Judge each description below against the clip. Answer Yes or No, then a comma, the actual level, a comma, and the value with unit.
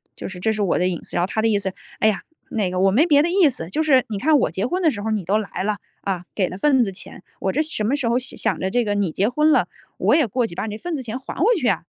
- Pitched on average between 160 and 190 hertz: No, high, 220 Hz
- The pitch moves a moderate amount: No, wide, 6.0 semitones